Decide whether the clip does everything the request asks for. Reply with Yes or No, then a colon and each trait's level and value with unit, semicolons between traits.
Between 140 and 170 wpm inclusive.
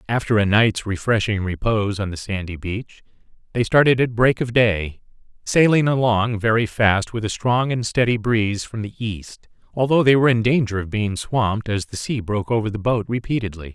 No: average, 190 wpm